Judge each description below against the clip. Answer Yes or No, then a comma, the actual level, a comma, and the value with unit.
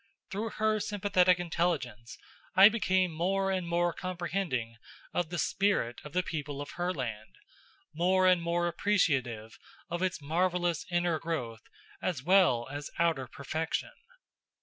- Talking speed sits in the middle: No, slow, 130 wpm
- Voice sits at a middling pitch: Yes, medium, 175 Hz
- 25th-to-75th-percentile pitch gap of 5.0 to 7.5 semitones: No, average, 4.2 semitones